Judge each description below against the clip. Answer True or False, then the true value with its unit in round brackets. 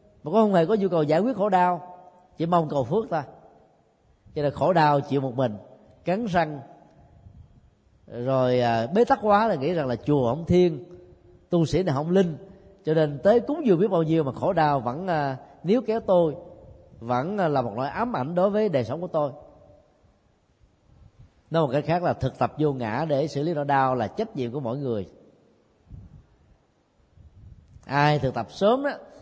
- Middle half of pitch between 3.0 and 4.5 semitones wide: False (5.5 semitones)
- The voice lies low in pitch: False (155 Hz)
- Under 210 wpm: True (190 wpm)